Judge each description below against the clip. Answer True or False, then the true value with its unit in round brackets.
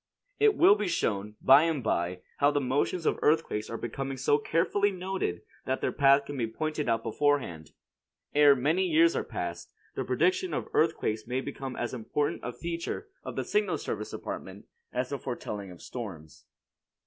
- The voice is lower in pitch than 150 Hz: True (140 Hz)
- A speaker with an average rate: True (175 wpm)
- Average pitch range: False (6.3 semitones)